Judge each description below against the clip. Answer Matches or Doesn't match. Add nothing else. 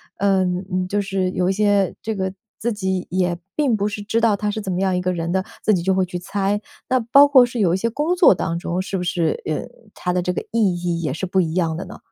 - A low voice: Doesn't match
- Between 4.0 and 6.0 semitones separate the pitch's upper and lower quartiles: Doesn't match